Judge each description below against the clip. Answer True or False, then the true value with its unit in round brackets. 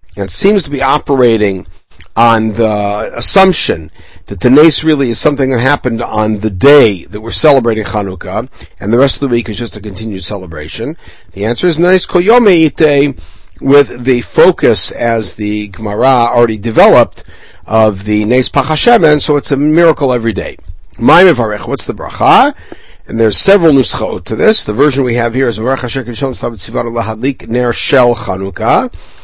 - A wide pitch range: False (4.8 semitones)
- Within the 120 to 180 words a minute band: True (160 wpm)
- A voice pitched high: False (120 Hz)